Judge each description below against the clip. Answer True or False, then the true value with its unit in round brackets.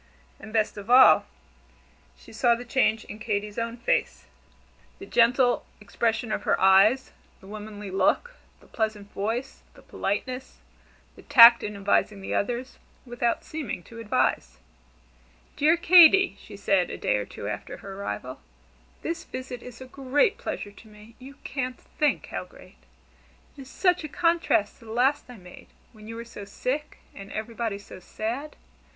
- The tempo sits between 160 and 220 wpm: True (165 wpm)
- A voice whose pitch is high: True (230 Hz)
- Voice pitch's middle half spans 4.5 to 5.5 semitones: False (4.1 semitones)